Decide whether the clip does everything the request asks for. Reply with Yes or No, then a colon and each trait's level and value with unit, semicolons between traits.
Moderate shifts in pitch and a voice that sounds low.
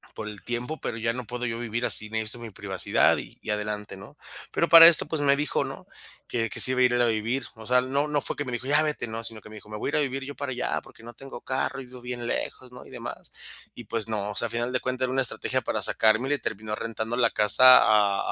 Yes: average, 3.2 semitones; low, 120 Hz